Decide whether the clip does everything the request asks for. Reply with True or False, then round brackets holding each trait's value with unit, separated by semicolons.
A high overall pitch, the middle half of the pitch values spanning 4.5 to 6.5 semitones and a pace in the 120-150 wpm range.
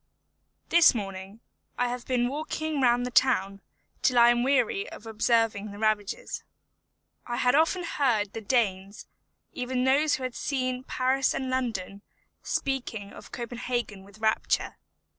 False (245 Hz; 3.6 semitones; 140 wpm)